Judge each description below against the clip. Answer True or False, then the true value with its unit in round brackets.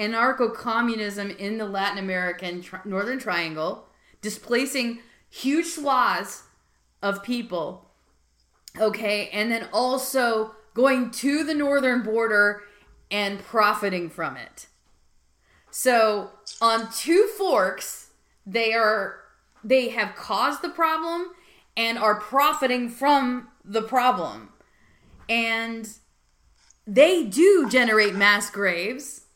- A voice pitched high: True (225 Hz)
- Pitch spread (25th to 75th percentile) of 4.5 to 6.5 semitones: False (4.0 semitones)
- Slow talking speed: True (105 wpm)